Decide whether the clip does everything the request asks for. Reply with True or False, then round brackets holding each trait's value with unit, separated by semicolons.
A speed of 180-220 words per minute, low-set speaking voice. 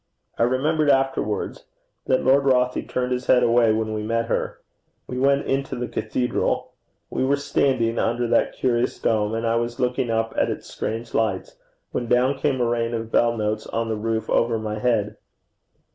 True (185 wpm; 120 Hz)